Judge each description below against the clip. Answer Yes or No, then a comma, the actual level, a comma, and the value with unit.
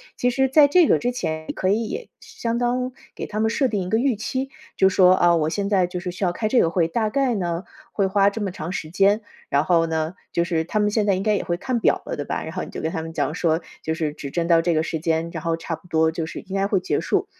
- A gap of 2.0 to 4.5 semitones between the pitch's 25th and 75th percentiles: No, average, 4.9 semitones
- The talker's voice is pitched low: No, medium, 185 Hz